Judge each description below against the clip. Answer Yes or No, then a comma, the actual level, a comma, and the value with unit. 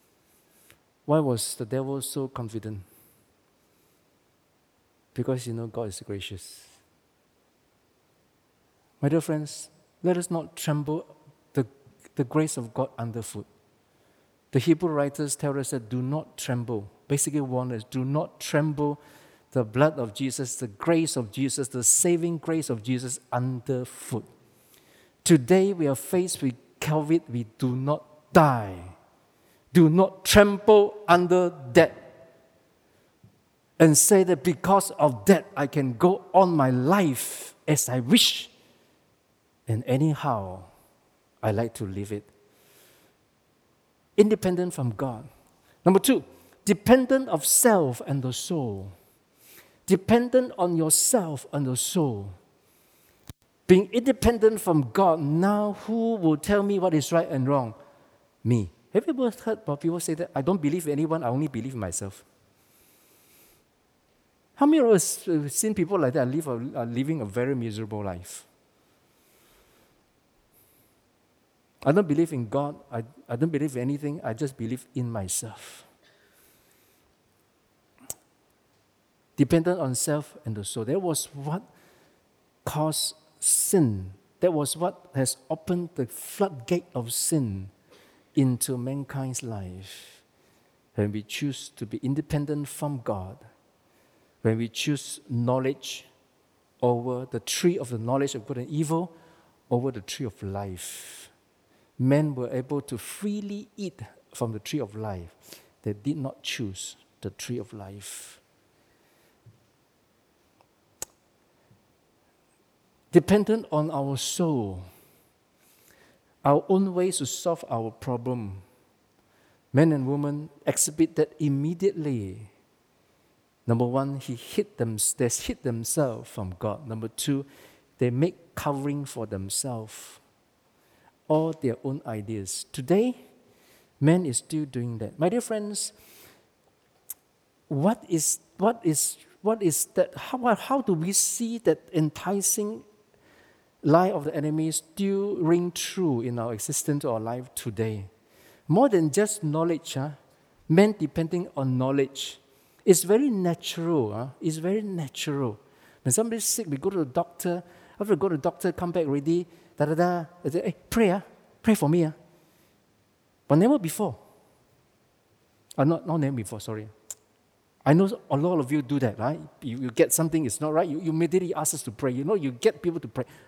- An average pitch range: No, wide, 5.9 semitones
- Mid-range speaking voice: Yes, medium, 145 Hz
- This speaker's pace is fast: No, average, 140 wpm